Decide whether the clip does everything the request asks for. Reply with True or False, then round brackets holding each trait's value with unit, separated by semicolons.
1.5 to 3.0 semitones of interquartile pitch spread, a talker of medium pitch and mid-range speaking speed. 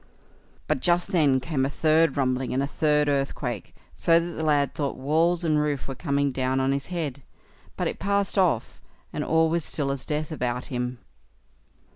False (3.4 semitones; 145 Hz; 185 wpm)